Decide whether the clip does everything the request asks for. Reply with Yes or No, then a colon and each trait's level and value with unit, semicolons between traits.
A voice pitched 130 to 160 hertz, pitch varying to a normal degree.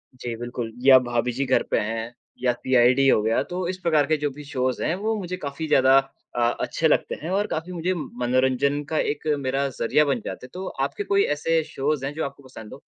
Yes: medium, 140 Hz; average, 3.9 semitones